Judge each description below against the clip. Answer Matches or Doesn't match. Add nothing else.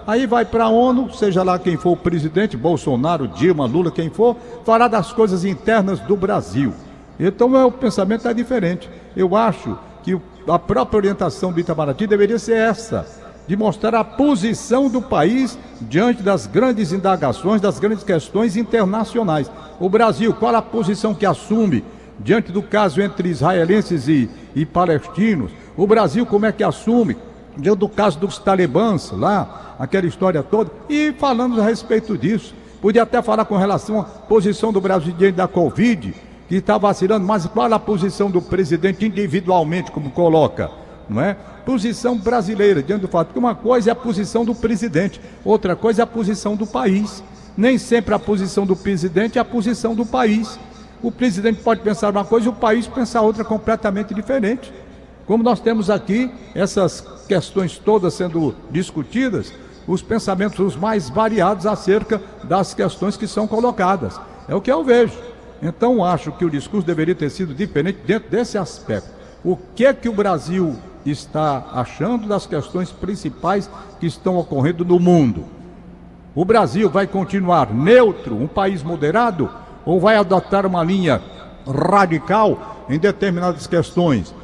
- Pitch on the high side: Matches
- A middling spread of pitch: Matches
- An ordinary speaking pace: Matches